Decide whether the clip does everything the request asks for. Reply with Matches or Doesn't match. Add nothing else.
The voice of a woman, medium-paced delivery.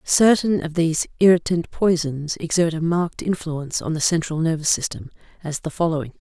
Matches